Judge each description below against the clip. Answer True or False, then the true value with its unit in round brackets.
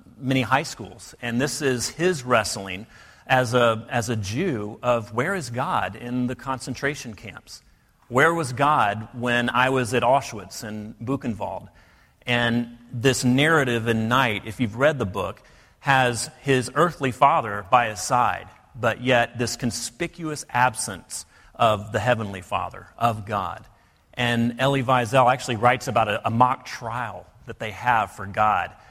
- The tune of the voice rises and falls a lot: False (2.7 semitones)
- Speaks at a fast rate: False (155 wpm)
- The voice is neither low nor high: False (120 Hz)